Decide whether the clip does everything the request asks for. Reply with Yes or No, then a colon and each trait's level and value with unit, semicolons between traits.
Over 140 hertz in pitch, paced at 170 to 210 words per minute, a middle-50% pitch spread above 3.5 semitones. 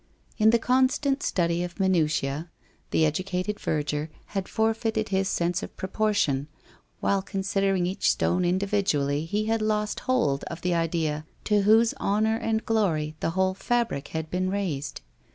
No: high, 190 Hz; average, 150 wpm; average, 4.8 semitones